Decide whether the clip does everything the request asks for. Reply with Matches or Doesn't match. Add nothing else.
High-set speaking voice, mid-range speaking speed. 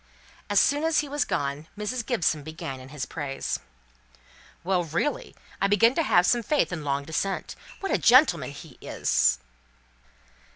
Doesn't match